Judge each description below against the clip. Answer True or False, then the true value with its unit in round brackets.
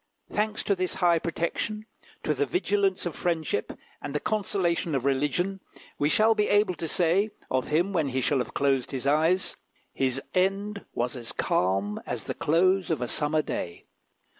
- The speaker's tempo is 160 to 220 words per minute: True (175 wpm)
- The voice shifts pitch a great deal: True (5.7 semitones)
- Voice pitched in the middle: True (165 Hz)